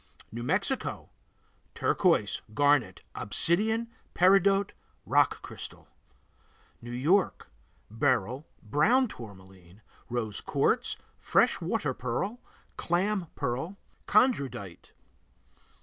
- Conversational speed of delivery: No, slow, 80 wpm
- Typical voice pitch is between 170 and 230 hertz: No, medium, 145 Hz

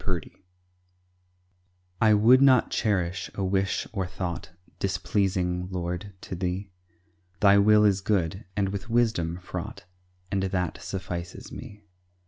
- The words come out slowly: Yes, slow, 125 wpm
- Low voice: Yes, very low, 95 Hz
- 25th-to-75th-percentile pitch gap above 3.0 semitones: No, narrow, 2.4 semitones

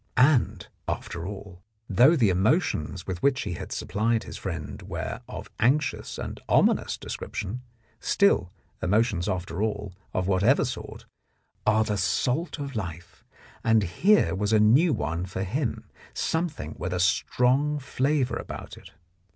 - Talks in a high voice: No, low, 110 Hz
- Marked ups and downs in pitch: Yes, wide, 6.3 semitones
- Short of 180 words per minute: Yes, average, 145 wpm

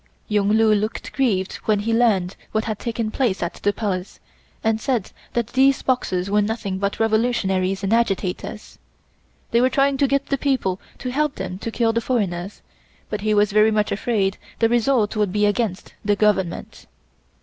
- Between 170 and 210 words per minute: Yes, average, 180 wpm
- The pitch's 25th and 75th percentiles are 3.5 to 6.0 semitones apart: No, average, 3.1 semitones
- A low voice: No, high, 215 Hz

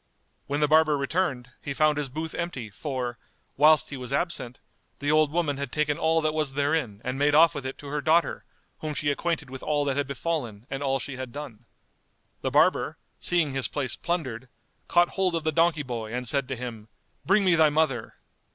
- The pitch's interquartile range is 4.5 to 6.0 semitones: No, average, 3.3 semitones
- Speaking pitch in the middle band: Yes, medium, 145 Hz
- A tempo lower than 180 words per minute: No, fast, 205 wpm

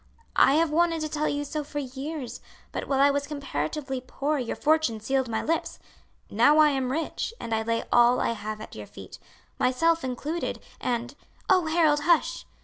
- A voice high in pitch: Yes, very high, 285 Hz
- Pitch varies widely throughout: No, average, 4.0 semitones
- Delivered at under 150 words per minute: No, average, 190 wpm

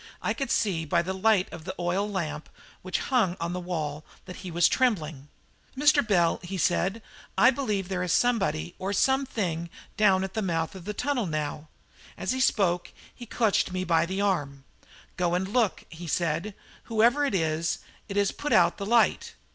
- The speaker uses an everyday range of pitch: Yes, average, 4.3 semitones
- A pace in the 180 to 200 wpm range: Yes, average, 185 wpm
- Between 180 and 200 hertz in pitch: Yes, medium, 185 Hz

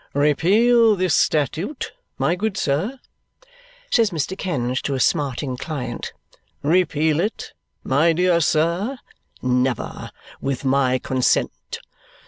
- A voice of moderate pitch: Yes, medium, 155 Hz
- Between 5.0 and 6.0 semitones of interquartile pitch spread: Yes, wide, 5.4 semitones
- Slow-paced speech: Yes, slow, 110 wpm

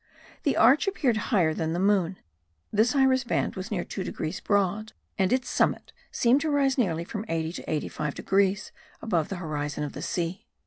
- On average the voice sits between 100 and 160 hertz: No, high, 195 Hz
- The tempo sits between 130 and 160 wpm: No, average, 185 wpm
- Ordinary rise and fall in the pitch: No, wide, 6.1 semitones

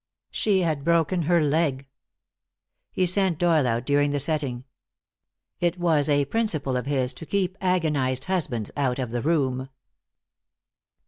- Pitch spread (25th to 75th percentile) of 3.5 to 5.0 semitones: Yes, average, 4.6 semitones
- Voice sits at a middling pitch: Yes, medium, 150 Hz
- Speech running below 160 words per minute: Yes, average, 140 wpm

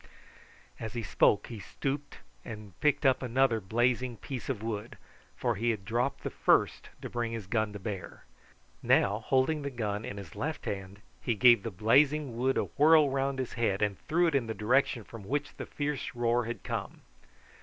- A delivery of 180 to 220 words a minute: Yes, average, 190 wpm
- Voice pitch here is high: No, low, 120 Hz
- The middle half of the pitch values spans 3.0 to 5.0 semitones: Yes, average, 4.1 semitones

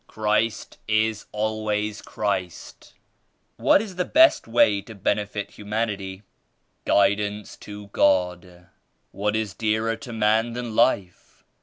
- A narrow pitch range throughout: Yes, narrow, 1.7 semitones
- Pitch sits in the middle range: No, low, 105 Hz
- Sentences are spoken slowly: Yes, slow, 115 wpm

